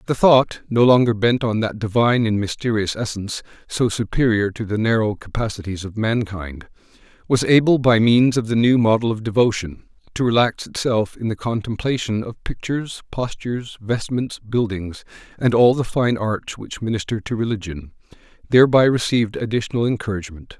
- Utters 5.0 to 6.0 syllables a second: Yes, 5.3 syllables/s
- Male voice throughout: Yes, male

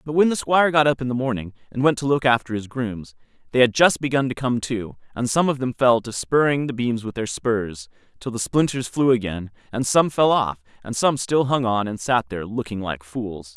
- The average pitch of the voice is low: Yes, low, 120 Hz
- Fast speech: Yes, fast, 245 wpm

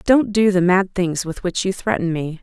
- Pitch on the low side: No, medium, 185 Hz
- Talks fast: Yes, fast, 250 wpm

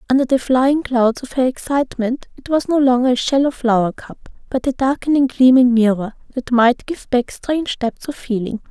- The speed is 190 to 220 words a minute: Yes, average, 195 wpm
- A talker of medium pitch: No, very high, 255 Hz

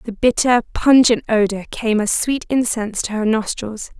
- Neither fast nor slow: Yes, average, 165 wpm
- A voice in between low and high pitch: No, high, 225 Hz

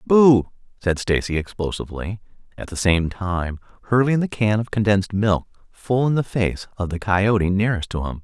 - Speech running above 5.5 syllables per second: No, 5.1 syllables/s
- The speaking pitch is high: No, low, 105 Hz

